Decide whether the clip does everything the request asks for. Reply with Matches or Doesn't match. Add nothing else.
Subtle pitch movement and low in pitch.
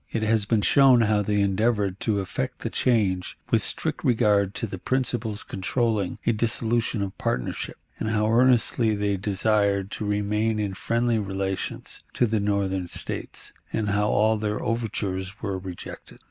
Matches